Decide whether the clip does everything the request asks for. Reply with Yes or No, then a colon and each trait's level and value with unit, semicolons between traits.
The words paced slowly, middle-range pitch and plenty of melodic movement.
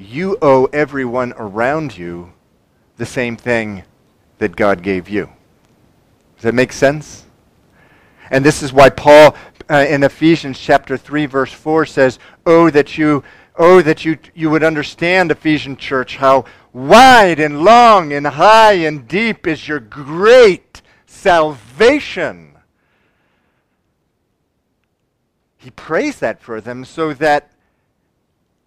No: slow, 125 wpm; medium, 145 Hz; average, 4.3 semitones